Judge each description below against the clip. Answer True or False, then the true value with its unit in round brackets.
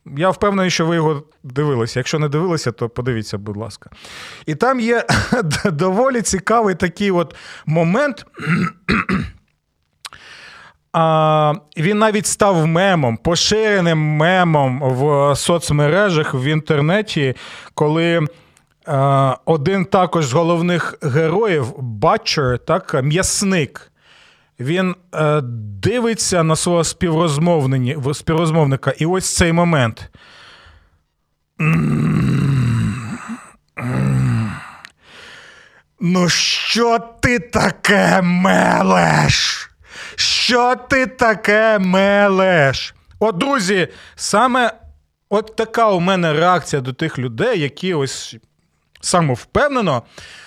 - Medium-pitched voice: True (160 Hz)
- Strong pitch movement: True (5.9 semitones)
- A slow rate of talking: True (85 wpm)